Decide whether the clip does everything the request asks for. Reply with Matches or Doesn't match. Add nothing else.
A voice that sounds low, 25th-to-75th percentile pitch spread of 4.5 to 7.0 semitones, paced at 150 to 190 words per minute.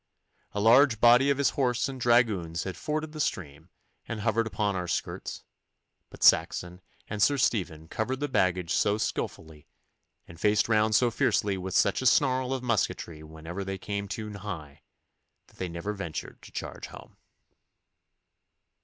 Matches